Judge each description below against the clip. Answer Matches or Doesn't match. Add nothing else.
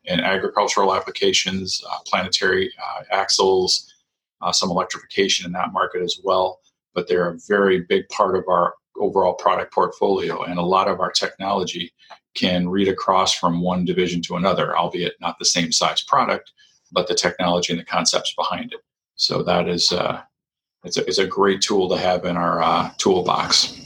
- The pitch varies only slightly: Matches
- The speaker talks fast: Doesn't match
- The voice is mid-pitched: Doesn't match